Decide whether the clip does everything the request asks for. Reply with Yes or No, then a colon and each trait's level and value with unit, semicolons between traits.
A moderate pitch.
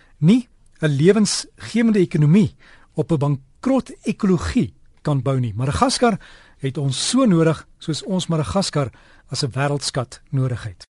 Yes: medium, 155 Hz